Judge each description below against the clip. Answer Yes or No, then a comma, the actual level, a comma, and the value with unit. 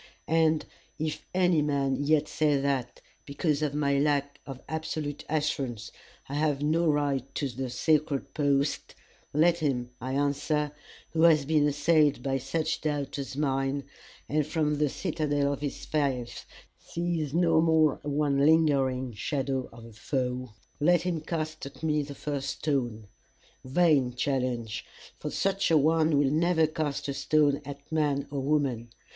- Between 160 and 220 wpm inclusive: No, average, 150 wpm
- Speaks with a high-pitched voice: No, medium, 145 Hz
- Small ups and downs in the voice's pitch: Yes, narrow, 2.3 semitones